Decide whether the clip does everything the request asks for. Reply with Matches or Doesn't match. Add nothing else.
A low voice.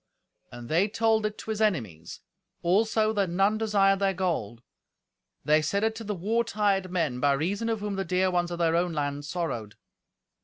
Doesn't match